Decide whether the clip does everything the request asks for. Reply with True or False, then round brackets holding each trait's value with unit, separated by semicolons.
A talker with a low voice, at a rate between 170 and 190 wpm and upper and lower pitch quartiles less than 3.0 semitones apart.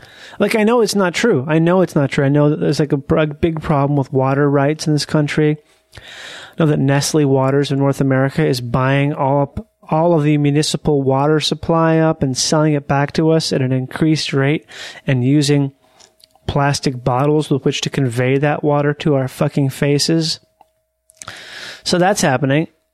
False (150 Hz; 185 wpm; 2.5 semitones)